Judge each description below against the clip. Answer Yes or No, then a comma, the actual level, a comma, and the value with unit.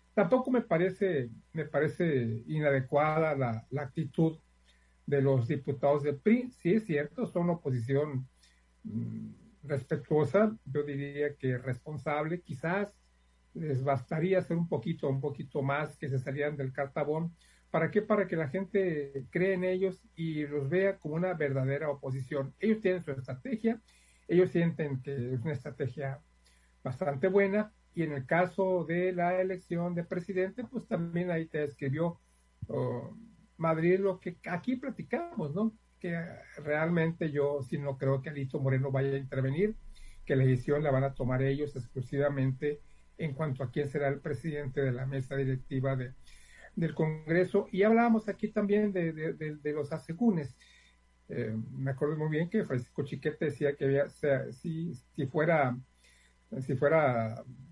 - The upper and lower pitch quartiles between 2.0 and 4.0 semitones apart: No, average, 4.6 semitones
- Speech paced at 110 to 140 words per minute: No, average, 160 wpm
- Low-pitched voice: No, medium, 150 Hz